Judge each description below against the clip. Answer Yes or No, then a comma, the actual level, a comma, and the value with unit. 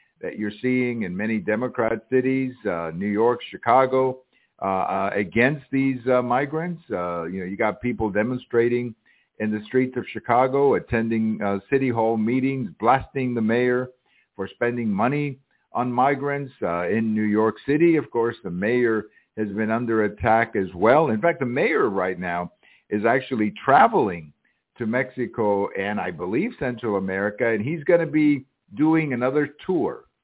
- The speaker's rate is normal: Yes, average, 160 wpm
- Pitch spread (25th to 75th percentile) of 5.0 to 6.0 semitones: No, average, 3.4 semitones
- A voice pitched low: Yes, low, 120 Hz